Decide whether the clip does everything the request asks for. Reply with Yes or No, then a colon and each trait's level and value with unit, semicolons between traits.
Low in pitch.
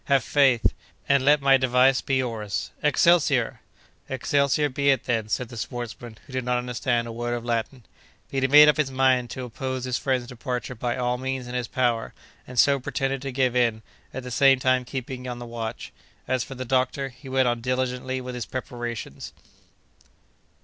Yes: low, 125 Hz